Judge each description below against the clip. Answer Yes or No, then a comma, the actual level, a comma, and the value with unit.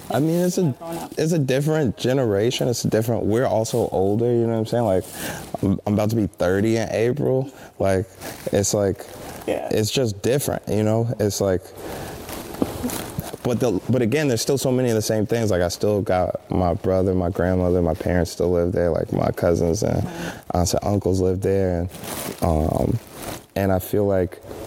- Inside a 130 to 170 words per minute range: No, average, 185 wpm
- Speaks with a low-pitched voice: Yes, low, 105 Hz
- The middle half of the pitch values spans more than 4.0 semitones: Yes, average, 4.4 semitones